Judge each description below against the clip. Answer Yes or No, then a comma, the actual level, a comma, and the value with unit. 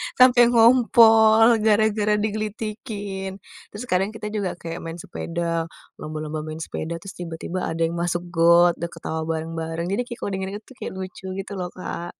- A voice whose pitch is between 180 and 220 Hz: Yes, high, 190 Hz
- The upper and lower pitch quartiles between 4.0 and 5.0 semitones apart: Yes, average, 4.5 semitones